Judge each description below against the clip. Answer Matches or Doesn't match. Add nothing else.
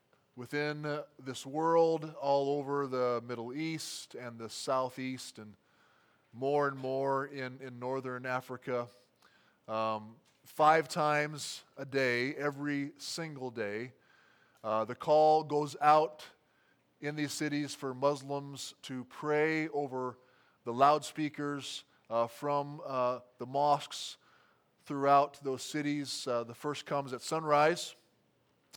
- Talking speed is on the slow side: Matches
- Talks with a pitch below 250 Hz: Matches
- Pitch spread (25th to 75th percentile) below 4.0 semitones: Matches